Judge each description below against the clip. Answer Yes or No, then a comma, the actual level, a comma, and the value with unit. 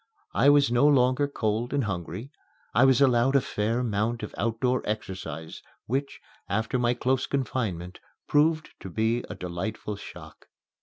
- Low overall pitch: Yes, low, 120 Hz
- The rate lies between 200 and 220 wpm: No, average, 150 wpm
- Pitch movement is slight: No, average, 4.2 semitones